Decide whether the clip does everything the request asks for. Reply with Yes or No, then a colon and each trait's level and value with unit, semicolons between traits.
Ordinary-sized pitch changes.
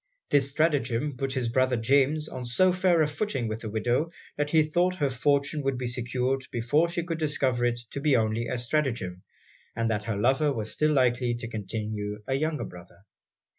Yes: average, 4.4 semitones